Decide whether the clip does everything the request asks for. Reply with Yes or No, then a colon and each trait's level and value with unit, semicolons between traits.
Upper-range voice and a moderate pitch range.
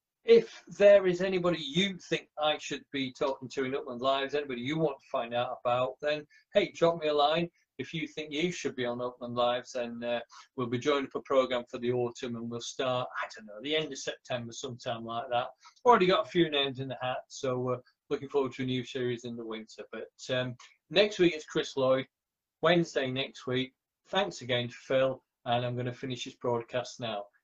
No: low, 130 Hz; average, 4.0 semitones